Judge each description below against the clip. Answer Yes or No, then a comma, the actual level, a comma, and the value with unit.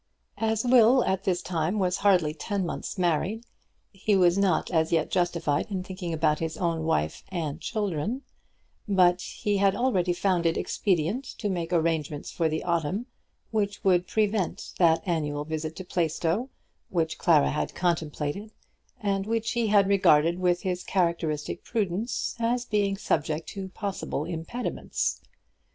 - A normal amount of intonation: Yes, average, 3.7 semitones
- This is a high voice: No, medium, 180 Hz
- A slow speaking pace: No, average, 150 wpm